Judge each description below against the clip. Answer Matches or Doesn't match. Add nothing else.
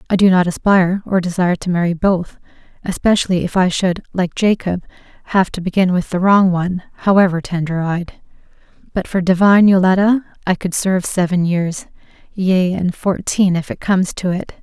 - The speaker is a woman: Matches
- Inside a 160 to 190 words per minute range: Matches